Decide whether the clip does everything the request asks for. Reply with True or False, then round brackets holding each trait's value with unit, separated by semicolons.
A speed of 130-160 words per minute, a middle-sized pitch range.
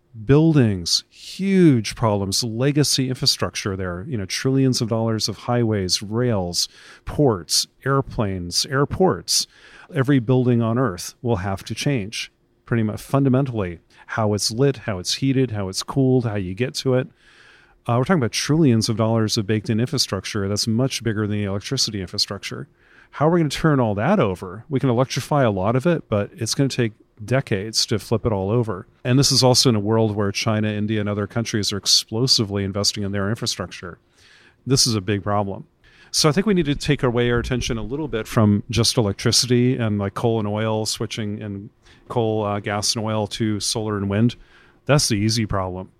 False (190 wpm; 3.8 semitones)